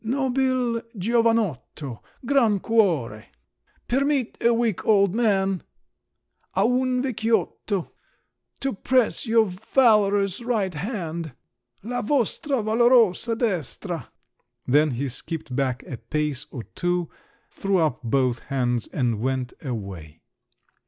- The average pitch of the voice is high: Yes, high, 195 Hz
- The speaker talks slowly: Yes, slow, 105 wpm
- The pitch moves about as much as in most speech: No, wide, 8.8 semitones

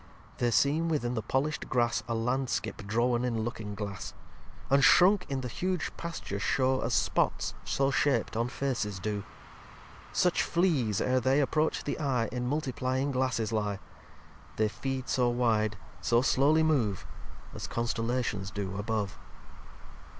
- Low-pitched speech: Yes, low, 125 Hz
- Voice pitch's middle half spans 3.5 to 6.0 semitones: Yes, average, 3.9 semitones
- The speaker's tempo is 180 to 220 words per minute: No, average, 145 wpm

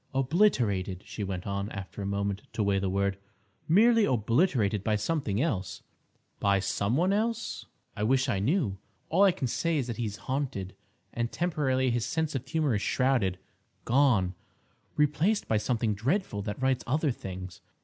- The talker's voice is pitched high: No, low, 120 Hz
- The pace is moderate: Yes, average, 160 wpm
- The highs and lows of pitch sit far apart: Yes, wide, 6.9 semitones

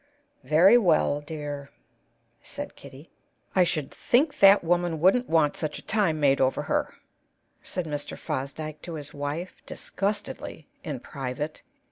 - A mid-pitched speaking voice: Yes, medium, 155 Hz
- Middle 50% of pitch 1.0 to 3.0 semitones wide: No, average, 3.8 semitones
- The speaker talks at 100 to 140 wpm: Yes, slow, 135 wpm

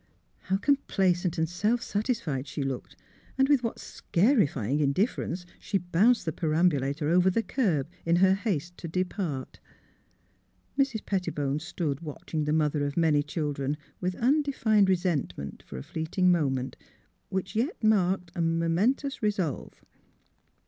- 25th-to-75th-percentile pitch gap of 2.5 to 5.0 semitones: No, wide, 5.5 semitones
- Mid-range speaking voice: Yes, medium, 175 Hz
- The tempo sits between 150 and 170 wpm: No, average, 140 wpm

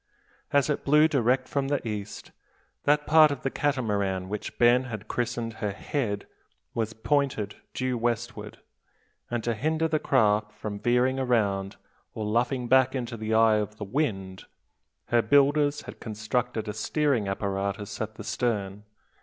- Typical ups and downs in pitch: Yes, average, 4.2 semitones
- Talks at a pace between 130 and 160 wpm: Yes, average, 155 wpm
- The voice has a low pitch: Yes, low, 115 Hz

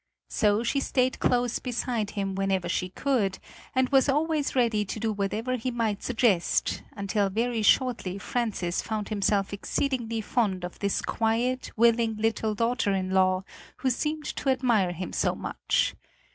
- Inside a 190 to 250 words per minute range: No, average, 155 wpm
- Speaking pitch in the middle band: No, high, 220 Hz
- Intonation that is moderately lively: Yes, average, 4.0 semitones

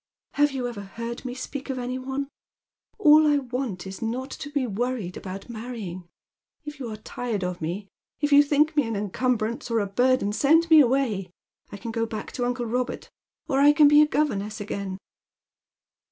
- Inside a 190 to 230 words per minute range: Yes, average, 195 wpm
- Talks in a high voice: Yes, high, 245 Hz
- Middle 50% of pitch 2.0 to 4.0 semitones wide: No, average, 4.9 semitones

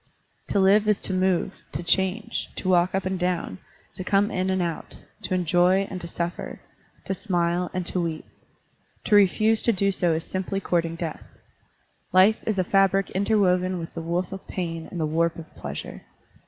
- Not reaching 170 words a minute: No, average, 185 wpm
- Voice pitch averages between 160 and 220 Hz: Yes, medium, 185 Hz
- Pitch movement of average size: No, narrow, 2.2 semitones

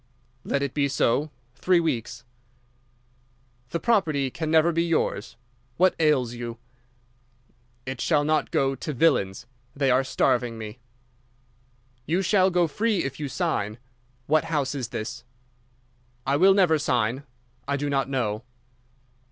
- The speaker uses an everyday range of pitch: Yes, average, 4.6 semitones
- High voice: No, medium, 140 Hz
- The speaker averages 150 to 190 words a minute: No, average, 140 wpm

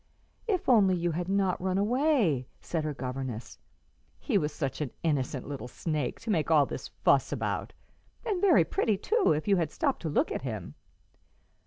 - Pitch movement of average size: No, wide, 7.2 semitones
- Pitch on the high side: No, medium, 170 Hz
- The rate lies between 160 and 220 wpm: Yes, average, 180 wpm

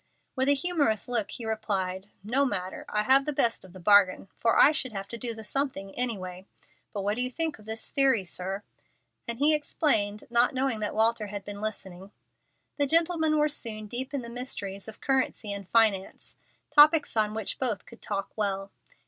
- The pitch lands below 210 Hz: No, high, 220 Hz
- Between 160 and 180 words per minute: No, average, 195 wpm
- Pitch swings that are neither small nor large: Yes, average, 4.8 semitones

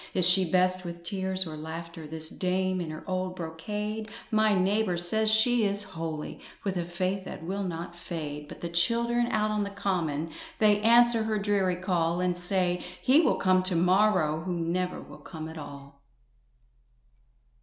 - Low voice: No, medium, 185 Hz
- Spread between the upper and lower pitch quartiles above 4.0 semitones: No, average, 3.5 semitones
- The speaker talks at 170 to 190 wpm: Yes, average, 175 wpm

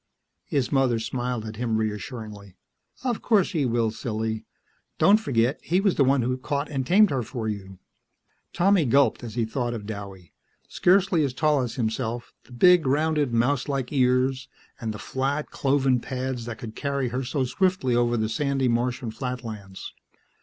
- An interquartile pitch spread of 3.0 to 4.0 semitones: Yes, average, 3.7 semitones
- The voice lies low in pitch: Yes, low, 125 Hz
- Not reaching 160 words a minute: No, average, 165 wpm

